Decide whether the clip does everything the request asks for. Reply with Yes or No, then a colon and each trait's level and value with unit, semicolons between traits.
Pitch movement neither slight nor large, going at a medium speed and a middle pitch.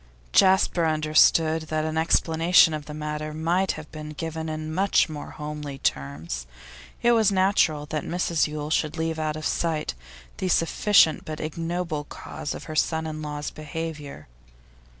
No: narrow, 1.5 semitones; average, 155 wpm; medium, 155 Hz